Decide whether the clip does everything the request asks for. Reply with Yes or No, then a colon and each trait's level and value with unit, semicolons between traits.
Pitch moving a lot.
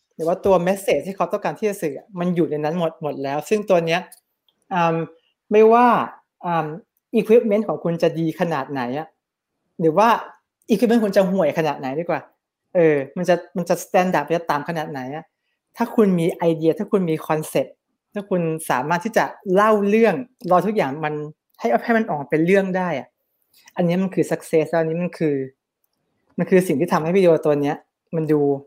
No: average, 4.1 semitones